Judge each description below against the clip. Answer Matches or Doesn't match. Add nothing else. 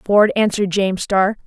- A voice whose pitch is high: Matches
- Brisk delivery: Doesn't match